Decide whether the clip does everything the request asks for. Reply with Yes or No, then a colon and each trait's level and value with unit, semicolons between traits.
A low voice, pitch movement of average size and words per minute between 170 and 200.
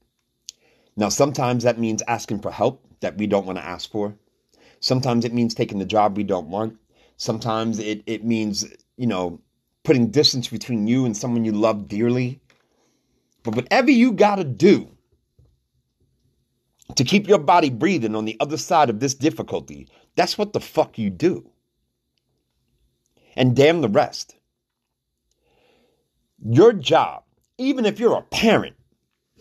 No: low, 120 Hz; average, 4.6 semitones; average, 150 wpm